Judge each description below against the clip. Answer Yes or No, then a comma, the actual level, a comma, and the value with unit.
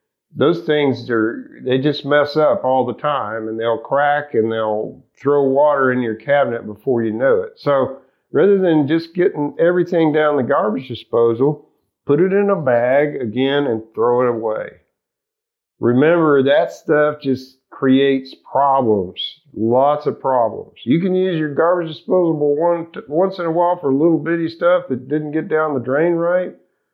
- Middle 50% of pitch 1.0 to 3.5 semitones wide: No, average, 4.6 semitones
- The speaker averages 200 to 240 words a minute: No, average, 165 wpm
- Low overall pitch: No, medium, 145 Hz